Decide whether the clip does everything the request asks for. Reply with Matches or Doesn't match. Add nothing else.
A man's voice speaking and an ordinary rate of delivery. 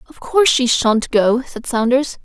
Doesn't match